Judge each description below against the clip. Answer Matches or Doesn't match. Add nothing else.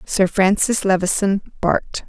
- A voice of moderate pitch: Doesn't match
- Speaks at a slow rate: Matches